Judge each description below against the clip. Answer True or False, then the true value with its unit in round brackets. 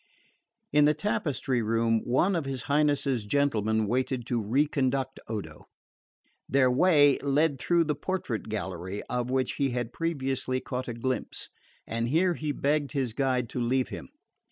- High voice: False (130 Hz)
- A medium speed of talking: True (155 wpm)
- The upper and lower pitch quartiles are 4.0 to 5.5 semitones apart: False (3.5 semitones)